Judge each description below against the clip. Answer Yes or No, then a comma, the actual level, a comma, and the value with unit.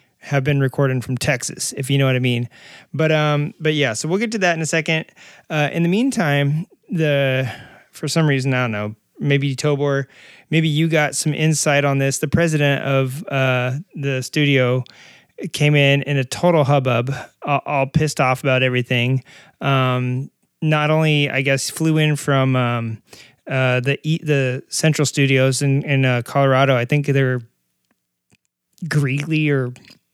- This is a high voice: No, medium, 140 Hz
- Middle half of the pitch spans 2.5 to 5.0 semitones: Yes, average, 2.8 semitones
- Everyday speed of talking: Yes, average, 170 wpm